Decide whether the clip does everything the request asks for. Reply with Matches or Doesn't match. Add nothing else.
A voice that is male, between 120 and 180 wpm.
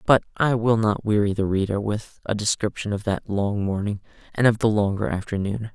Doesn't match